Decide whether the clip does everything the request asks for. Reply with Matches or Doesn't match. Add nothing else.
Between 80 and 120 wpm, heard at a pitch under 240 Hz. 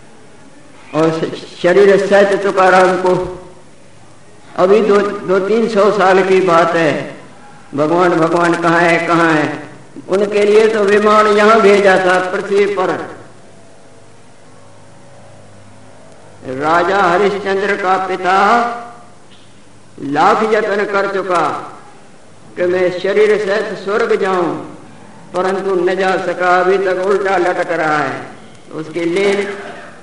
Matches